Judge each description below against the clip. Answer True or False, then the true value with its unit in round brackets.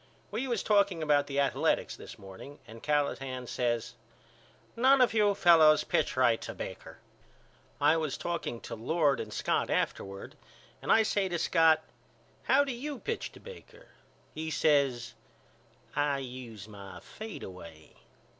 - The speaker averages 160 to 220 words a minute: False (145 wpm)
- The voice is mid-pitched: True (150 Hz)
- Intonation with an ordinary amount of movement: False (9.0 semitones)